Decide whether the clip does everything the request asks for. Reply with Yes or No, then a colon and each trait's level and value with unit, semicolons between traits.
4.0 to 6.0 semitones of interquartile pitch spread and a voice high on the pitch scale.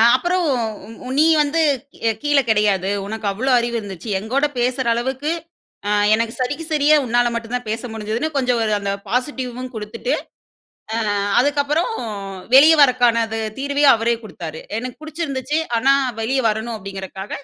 Yes: average, 4.3 semitones; high, 245 Hz